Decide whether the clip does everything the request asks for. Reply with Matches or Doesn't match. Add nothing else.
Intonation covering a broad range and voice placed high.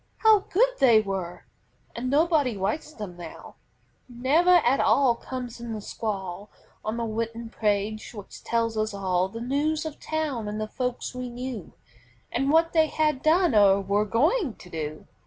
Matches